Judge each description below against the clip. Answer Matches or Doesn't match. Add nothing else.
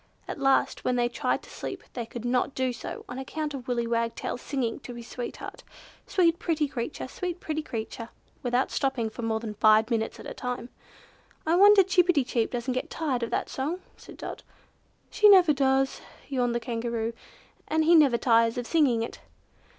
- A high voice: Matches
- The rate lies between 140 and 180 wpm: Doesn't match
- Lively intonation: Doesn't match